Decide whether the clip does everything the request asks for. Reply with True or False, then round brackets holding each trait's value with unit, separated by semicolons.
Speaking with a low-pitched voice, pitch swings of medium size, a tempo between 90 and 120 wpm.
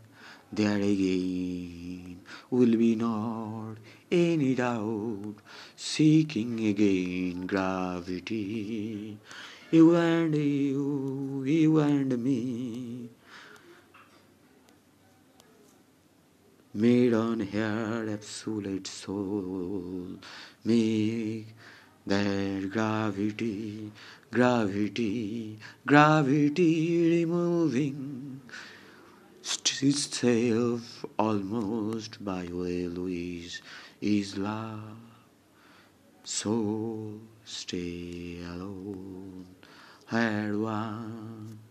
False (110 Hz; 3.6 semitones; 60 wpm)